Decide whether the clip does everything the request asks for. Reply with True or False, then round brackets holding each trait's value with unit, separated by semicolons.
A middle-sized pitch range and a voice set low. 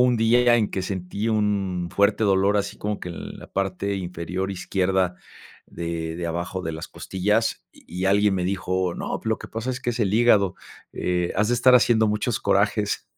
True (3.2 semitones; 100 Hz)